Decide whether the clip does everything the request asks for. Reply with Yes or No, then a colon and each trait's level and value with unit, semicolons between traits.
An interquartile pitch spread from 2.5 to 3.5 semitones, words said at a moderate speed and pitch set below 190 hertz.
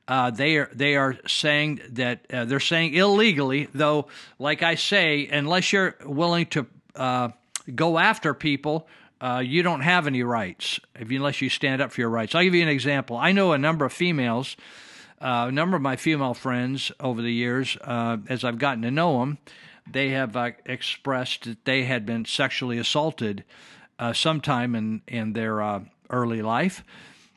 No: average, 4.2 semitones; average, 185 wpm; low, 135 Hz